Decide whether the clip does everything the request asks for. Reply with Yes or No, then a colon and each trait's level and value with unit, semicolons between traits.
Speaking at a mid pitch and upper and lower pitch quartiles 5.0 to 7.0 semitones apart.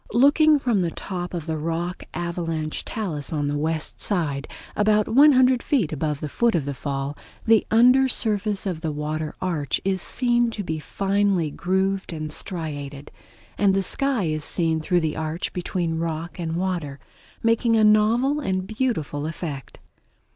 Yes: medium, 175 Hz; wide, 5.5 semitones